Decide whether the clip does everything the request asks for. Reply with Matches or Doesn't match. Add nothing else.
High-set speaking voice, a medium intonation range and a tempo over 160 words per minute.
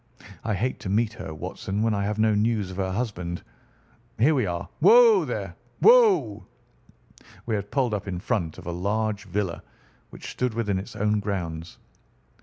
Doesn't match